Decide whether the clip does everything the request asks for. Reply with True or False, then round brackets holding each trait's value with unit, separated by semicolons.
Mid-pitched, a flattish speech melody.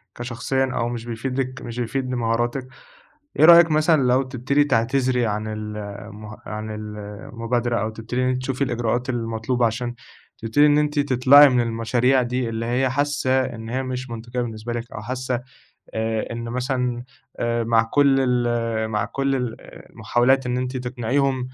False (125 Hz; 2.3 semitones)